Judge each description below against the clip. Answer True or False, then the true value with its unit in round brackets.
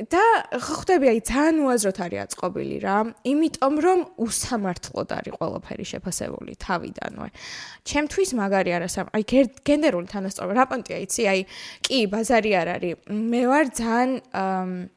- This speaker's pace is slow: True (130 wpm)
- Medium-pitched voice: False (230 Hz)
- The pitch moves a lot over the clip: True (6.0 semitones)